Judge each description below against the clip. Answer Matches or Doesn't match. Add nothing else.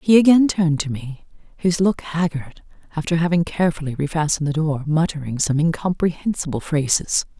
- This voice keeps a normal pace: Matches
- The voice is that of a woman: Matches